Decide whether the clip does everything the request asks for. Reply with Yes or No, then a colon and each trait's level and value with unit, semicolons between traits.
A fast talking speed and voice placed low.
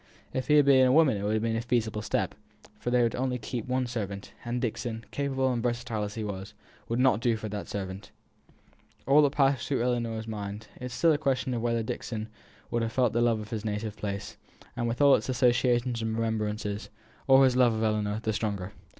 Yes: fast, 225 wpm; low, 115 Hz